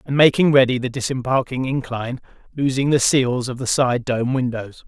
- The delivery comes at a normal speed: Yes, average, 170 wpm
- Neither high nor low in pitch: No, low, 130 Hz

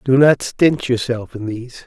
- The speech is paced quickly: No, average, 195 wpm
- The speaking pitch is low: Yes, low, 125 Hz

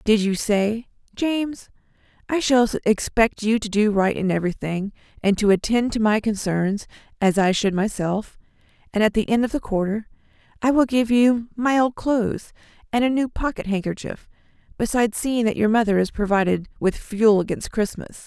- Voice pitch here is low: No, high, 220 Hz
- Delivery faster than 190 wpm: No, average, 175 wpm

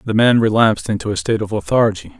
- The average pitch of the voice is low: Yes, low, 105 Hz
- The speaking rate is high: Yes, fast, 220 wpm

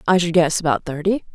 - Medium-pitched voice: Yes, medium, 170 Hz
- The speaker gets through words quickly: Yes, fast, 225 wpm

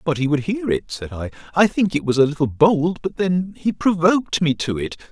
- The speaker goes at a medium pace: No, fast, 245 wpm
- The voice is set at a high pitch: No, medium, 160 Hz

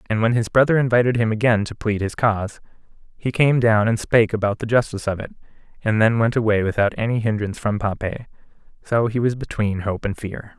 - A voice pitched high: No, low, 110 Hz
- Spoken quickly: Yes, fast, 210 wpm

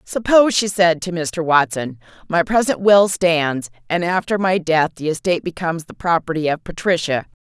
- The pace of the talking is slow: No, average, 170 wpm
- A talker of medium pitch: Yes, medium, 170 Hz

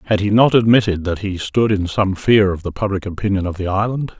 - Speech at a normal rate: No, fast, 245 wpm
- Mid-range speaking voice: No, low, 100 Hz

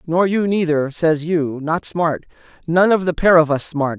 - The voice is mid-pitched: Yes, medium, 165 Hz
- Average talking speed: Yes, average, 195 wpm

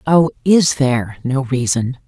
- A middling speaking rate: Yes, average, 145 wpm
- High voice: No, low, 135 Hz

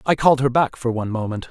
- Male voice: Yes, male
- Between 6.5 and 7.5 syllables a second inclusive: Yes, 7.2 syllables/s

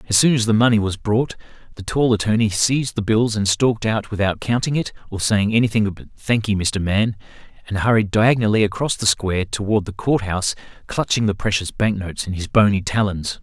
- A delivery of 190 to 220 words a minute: Yes, average, 195 wpm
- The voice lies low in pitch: Yes, low, 105 Hz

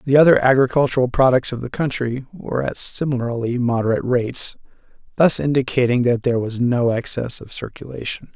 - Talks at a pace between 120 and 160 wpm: Yes, average, 150 wpm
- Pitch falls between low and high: No, low, 125 Hz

